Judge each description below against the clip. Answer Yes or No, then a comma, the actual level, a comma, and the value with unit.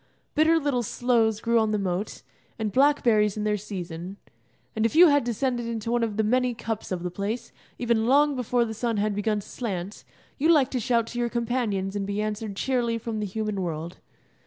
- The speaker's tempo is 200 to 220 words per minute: Yes, fast, 205 wpm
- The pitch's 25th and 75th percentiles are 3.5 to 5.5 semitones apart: No, average, 2.9 semitones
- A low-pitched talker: No, high, 225 Hz